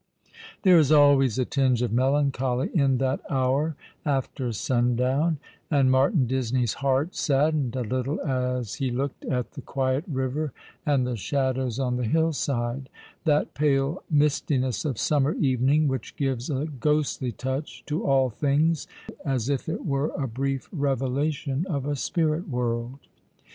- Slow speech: No, average, 150 wpm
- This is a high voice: No, low, 135 Hz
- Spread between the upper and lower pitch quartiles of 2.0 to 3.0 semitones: Yes, narrow, 2.4 semitones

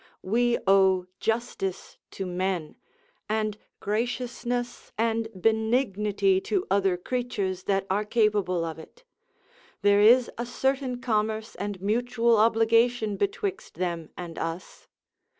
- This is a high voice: Yes, high, 220 Hz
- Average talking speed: No, slow, 115 wpm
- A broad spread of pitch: No, average, 3.9 semitones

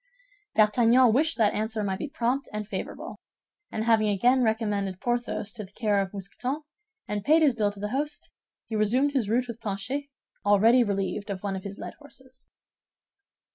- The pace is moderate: Yes, average, 175 wpm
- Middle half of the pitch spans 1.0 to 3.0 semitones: No, average, 3.8 semitones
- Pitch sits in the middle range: No, high, 220 Hz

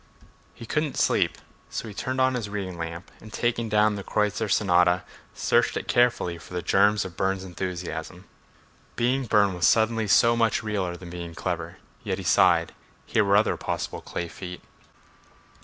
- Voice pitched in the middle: No, low, 100 Hz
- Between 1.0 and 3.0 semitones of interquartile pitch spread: No, average, 4.1 semitones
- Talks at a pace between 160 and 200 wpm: Yes, average, 175 wpm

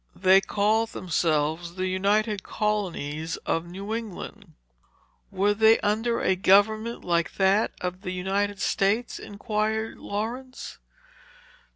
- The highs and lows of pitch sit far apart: No, average, 2.8 semitones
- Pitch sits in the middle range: No, high, 200 Hz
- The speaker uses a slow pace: Yes, slow, 110 wpm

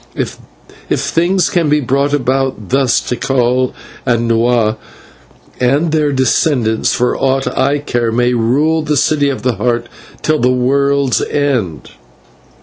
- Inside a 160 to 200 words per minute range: No, average, 140 wpm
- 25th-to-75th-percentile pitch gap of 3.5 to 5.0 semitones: No, average, 3.0 semitones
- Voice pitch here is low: Yes, low, 130 Hz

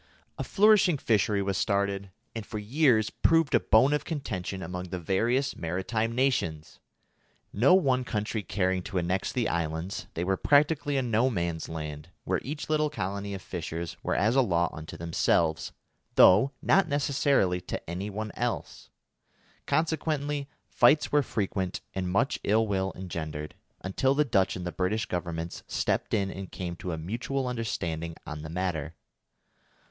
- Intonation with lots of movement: Yes, wide, 6.9 semitones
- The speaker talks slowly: No, average, 160 wpm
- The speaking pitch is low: Yes, low, 100 Hz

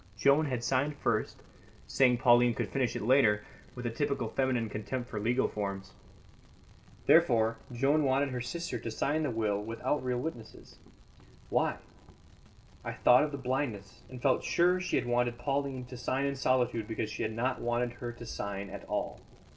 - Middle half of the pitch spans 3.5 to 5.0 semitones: No, average, 3.1 semitones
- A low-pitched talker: Yes, low, 125 Hz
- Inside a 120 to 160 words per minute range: No, average, 175 wpm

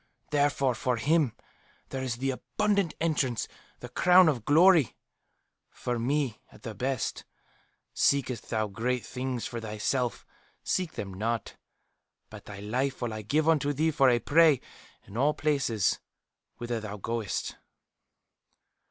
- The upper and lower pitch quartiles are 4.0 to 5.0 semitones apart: Yes, average, 4.3 semitones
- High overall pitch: No, low, 130 Hz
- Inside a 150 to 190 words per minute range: No, slow, 135 wpm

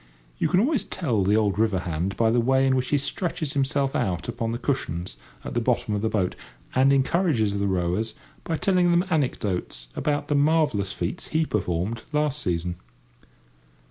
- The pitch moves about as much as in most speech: No, wide, 6.8 semitones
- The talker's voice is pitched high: No, low, 120 Hz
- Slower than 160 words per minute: No, average, 180 wpm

